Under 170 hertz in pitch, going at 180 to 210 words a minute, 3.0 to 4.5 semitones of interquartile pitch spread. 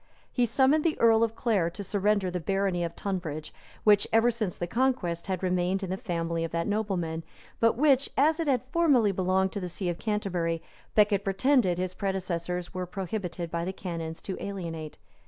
No: high, 190 Hz; average, 190 wpm; average, 4.2 semitones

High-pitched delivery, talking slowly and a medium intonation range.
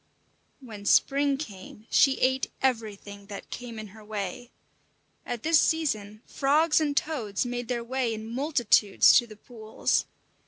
No: high, 240 Hz; average, 145 wpm; average, 4.1 semitones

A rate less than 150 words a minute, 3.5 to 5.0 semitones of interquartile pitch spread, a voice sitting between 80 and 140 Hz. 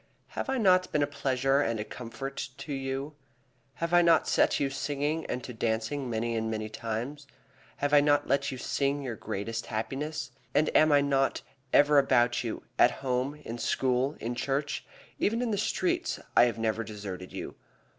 No: average, 185 wpm; average, 3.9 semitones; low, 135 Hz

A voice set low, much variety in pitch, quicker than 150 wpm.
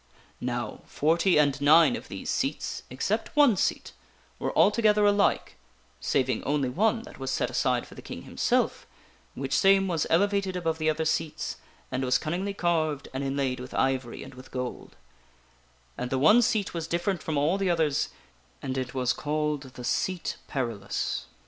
No: medium, 155 Hz; wide, 5.9 semitones; average, 170 wpm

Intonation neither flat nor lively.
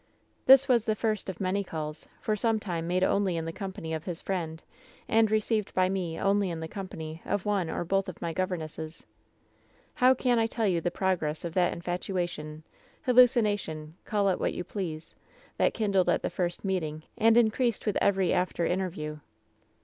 Yes: average, 4.1 semitones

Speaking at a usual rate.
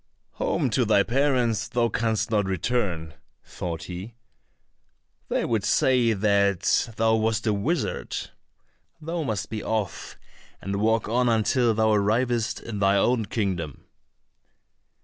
No: slow, 130 wpm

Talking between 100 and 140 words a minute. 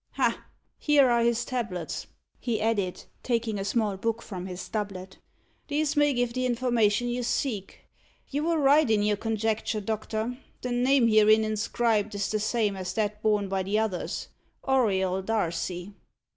No: average, 160 wpm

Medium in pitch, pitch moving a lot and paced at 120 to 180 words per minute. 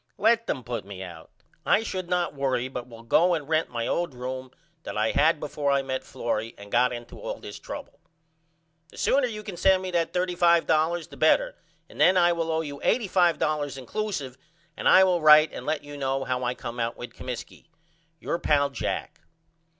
No: medium, 150 Hz; wide, 5.7 semitones; average, 195 wpm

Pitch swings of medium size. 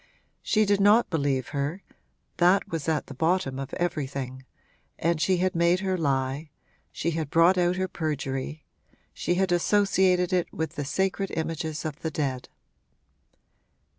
Yes: average, 4.3 semitones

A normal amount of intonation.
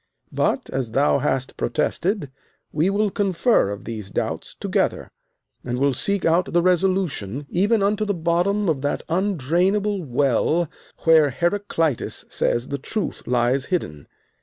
No: wide, 6.5 semitones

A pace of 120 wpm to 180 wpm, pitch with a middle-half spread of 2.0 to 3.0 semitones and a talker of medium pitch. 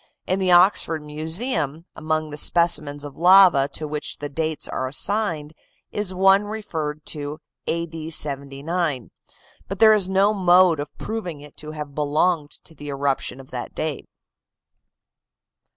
No: average, 150 wpm; average, 3.8 semitones; medium, 155 Hz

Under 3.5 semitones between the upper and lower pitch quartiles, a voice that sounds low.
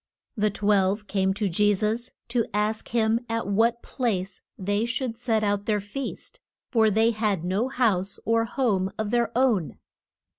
No: narrow, 2.4 semitones; high, 215 Hz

